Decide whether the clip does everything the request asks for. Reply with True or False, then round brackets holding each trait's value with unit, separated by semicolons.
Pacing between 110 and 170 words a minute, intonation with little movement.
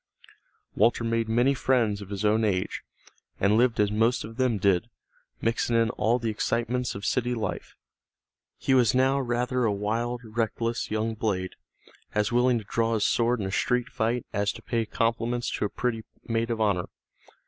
False (180 wpm; 2.2 semitones)